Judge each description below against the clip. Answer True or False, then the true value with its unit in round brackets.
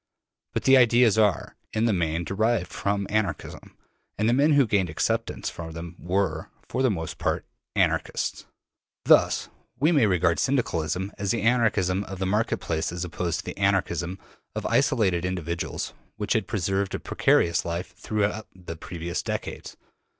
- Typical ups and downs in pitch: True (4.2 semitones)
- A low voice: True (95 Hz)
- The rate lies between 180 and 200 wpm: False (160 wpm)